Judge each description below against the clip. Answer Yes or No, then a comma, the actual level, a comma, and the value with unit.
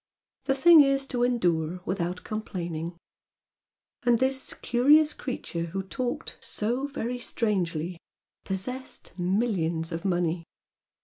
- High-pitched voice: Yes, high, 205 Hz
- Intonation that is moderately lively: No, wide, 6.6 semitones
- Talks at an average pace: No, slow, 110 wpm